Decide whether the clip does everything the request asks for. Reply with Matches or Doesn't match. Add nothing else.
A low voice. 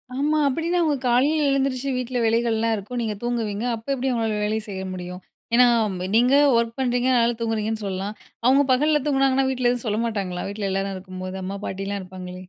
Doesn't match